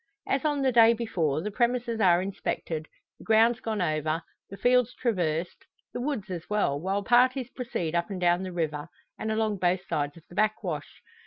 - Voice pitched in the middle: No, high, 200 Hz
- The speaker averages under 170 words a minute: No, average, 185 wpm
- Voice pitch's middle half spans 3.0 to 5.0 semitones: No, wide, 5.5 semitones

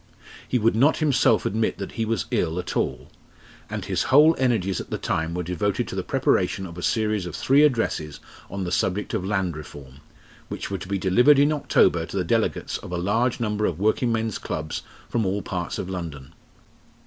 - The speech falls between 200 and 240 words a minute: Yes, fast, 205 wpm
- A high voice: No, low, 100 Hz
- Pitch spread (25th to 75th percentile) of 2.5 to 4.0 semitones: No, average, 4.5 semitones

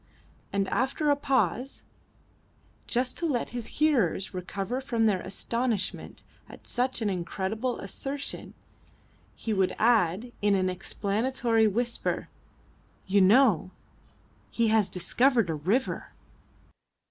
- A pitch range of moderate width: Yes, average, 4.6 semitones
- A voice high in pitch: Yes, high, 225 Hz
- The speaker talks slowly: Yes, slow, 110 wpm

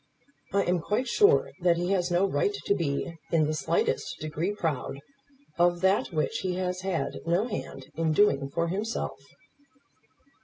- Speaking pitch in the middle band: Yes, medium, 175 Hz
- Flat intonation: No, average, 3.5 semitones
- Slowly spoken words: No, average, 160 wpm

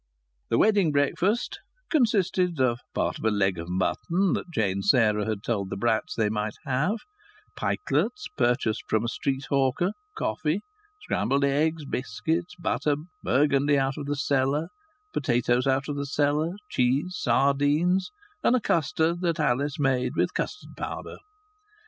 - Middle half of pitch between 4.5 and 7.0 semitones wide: Yes, average, 5.1 semitones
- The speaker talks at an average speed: Yes, average, 145 wpm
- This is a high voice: No, medium, 140 Hz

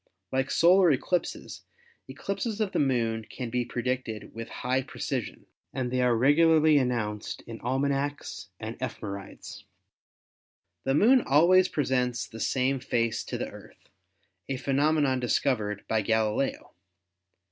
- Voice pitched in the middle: No, low, 130 Hz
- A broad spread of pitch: No, average, 3.8 semitones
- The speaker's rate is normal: No, slow, 125 wpm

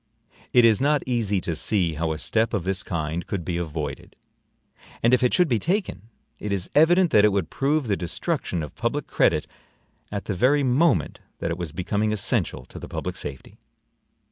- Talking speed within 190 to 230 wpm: Yes, average, 195 wpm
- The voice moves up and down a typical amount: No, wide, 6.7 semitones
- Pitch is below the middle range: Yes, low, 105 Hz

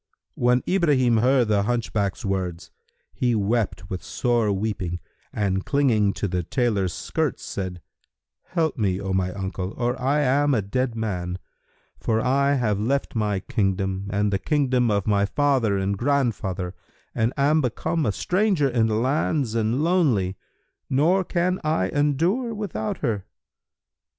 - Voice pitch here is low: Yes, low, 115 Hz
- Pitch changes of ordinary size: No, wide, 6.0 semitones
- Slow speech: No, average, 145 wpm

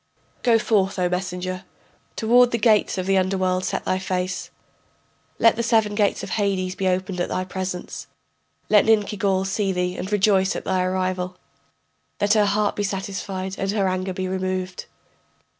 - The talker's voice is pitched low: No, high, 190 Hz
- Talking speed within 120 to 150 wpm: No, average, 170 wpm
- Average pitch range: No, narrow, 1.9 semitones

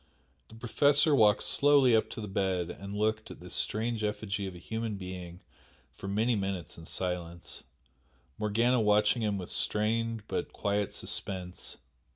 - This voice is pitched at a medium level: No, low, 105 Hz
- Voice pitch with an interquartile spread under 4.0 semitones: Yes, average, 2.9 semitones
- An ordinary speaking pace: Yes, average, 155 wpm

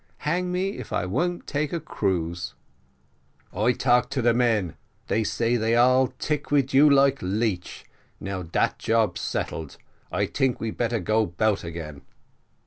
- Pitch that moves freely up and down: Yes, wide, 6.5 semitones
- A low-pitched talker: Yes, low, 115 Hz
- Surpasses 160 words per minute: No, average, 155 wpm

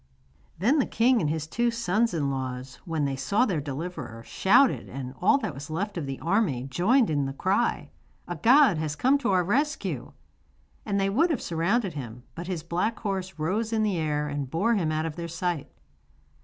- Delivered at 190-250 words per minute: Yes, average, 200 wpm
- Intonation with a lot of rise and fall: Yes, wide, 7.0 semitones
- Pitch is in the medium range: Yes, medium, 175 Hz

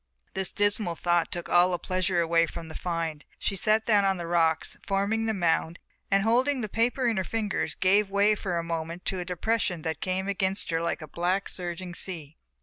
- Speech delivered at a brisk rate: Yes, fast, 210 wpm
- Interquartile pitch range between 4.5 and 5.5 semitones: No, average, 3.2 semitones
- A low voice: No, medium, 185 Hz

